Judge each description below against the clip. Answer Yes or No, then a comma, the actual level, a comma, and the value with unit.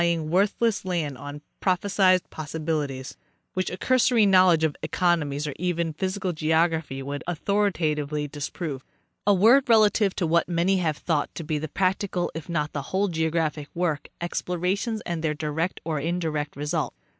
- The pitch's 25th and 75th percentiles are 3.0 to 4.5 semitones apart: Yes, average, 3.5 semitones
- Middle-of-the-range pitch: Yes, medium, 165 Hz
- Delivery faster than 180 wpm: No, average, 170 wpm